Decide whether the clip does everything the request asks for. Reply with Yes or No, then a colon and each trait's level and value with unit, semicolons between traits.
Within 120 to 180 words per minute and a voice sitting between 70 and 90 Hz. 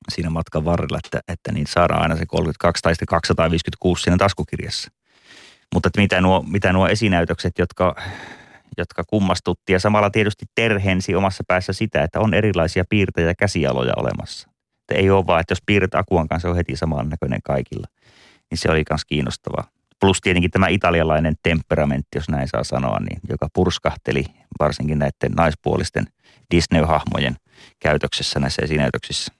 Yes: fast, 155 wpm; very low, 85 Hz